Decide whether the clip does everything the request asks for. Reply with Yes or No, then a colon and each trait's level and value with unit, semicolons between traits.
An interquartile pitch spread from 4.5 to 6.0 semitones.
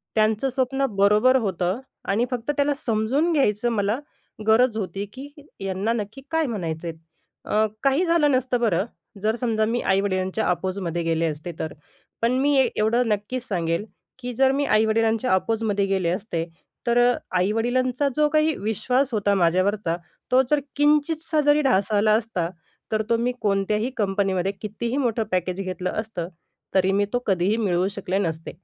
Yes: average, 4.8 semitones